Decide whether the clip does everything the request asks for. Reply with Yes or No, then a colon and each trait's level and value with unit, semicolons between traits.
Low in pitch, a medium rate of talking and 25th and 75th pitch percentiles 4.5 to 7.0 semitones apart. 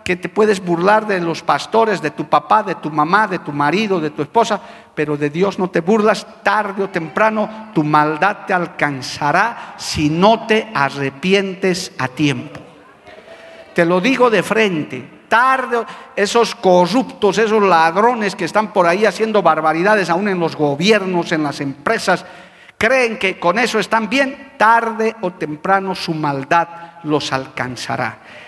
No: medium, 185 Hz; average, 155 wpm; average, 5.1 semitones